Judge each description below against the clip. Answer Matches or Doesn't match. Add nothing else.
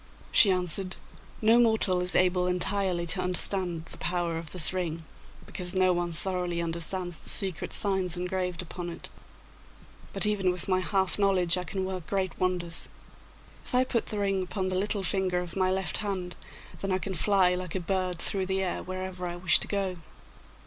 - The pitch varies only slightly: Matches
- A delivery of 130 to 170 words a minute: Doesn't match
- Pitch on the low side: Doesn't match